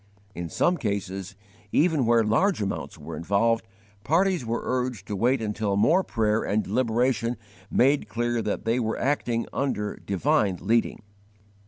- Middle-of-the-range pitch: No, low, 115 Hz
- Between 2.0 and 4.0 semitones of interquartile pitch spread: Yes, average, 3.6 semitones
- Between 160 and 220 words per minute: No, average, 145 wpm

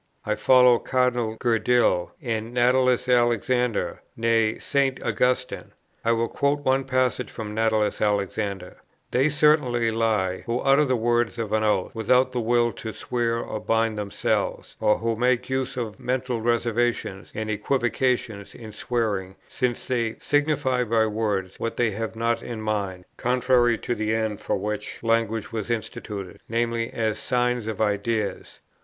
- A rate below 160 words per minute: Yes, average, 150 wpm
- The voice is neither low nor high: No, low, 115 Hz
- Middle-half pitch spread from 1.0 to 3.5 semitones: Yes, narrow, 2.4 semitones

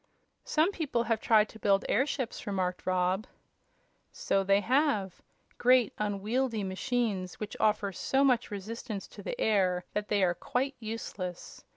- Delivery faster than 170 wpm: No, average, 145 wpm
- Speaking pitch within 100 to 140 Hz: No, high, 215 Hz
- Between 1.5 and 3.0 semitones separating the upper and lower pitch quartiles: No, average, 4.1 semitones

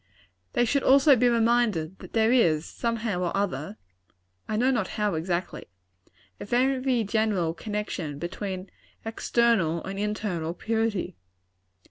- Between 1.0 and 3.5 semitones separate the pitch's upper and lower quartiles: No, average, 4.9 semitones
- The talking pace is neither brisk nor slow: No, slow, 125 wpm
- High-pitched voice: Yes, high, 210 Hz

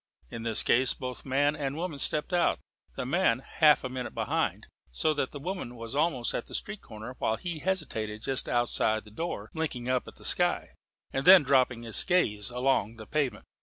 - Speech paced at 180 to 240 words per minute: Yes, average, 200 wpm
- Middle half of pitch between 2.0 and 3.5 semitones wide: No, average, 4.9 semitones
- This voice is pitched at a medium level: No, low, 130 Hz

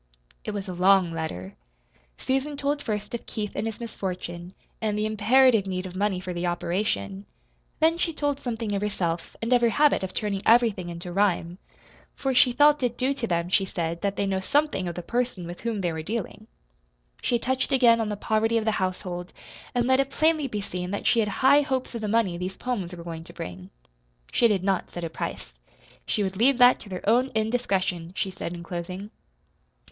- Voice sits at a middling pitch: No, high, 205 Hz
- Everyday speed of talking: No, fast, 210 wpm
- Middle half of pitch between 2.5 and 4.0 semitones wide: No, average, 5.0 semitones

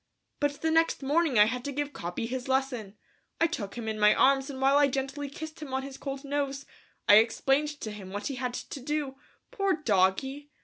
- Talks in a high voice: Yes, very high, 270 Hz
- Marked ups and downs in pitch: No, average, 3.5 semitones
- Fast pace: Yes, fast, 215 wpm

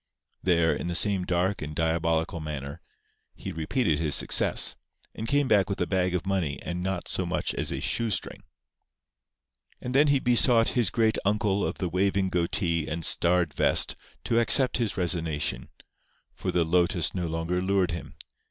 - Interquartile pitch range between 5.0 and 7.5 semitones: No, average, 3.6 semitones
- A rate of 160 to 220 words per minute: Yes, average, 170 wpm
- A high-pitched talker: No, very low, 90 Hz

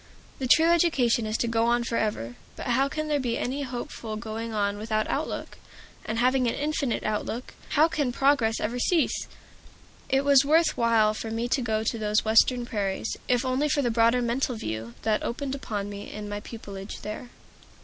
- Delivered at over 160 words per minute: Yes, average, 190 wpm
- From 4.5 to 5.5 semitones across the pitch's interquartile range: No, average, 3.6 semitones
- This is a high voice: Yes, high, 235 Hz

